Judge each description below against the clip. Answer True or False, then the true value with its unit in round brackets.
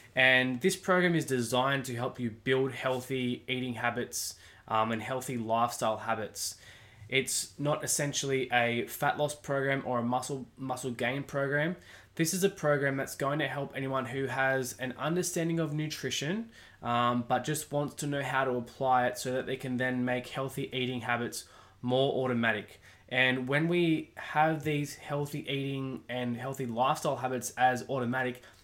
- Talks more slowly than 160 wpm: False (165 wpm)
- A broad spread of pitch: False (2.6 semitones)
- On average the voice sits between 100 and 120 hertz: False (130 Hz)